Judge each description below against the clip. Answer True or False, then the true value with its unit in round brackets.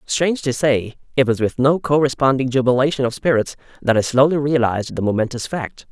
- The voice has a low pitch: True (130 Hz)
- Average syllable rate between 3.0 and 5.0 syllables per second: False (5.8 syllables/s)